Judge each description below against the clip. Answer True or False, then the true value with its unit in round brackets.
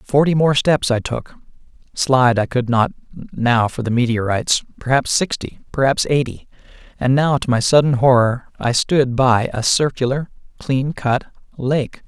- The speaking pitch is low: True (130 Hz)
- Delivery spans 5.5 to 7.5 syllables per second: False (3.9 syllables/s)